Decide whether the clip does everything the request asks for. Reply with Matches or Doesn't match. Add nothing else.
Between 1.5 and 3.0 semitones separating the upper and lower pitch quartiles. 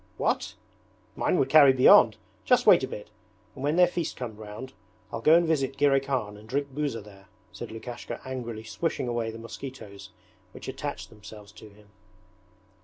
Doesn't match